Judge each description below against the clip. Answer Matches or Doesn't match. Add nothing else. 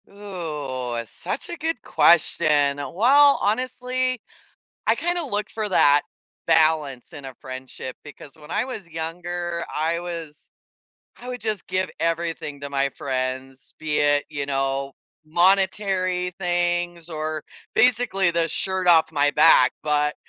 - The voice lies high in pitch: Doesn't match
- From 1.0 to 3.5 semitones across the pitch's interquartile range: Doesn't match